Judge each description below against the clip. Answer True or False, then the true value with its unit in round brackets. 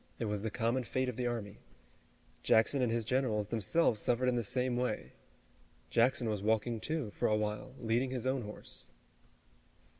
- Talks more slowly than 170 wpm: False (175 wpm)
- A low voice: True (115 Hz)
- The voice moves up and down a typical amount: True (3.0 semitones)